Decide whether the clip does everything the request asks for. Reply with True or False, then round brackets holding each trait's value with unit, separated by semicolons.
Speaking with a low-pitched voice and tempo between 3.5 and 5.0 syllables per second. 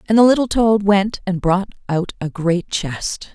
False (195 Hz; 4.2 syllables/s)